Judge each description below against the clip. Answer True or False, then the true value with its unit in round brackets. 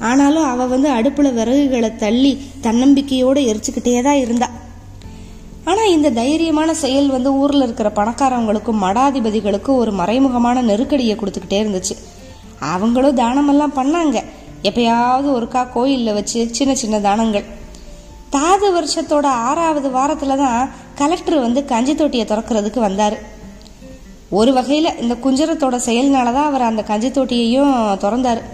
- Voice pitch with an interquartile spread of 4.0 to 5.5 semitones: True (4.5 semitones)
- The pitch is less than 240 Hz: False (250 Hz)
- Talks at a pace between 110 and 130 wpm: True (115 wpm)